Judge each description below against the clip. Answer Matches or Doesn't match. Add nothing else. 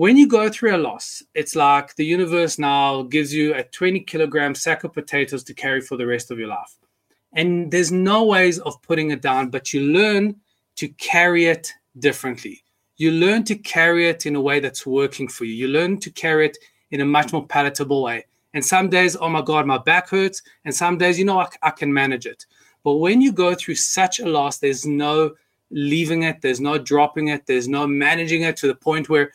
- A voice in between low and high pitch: Matches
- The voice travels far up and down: Doesn't match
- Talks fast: Matches